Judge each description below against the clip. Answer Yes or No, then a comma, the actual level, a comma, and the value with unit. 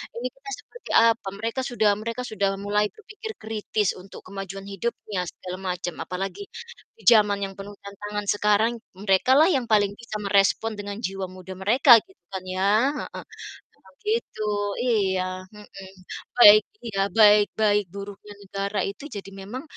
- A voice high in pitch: Yes, high, 205 Hz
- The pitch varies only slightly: Yes, narrow, 2.3 semitones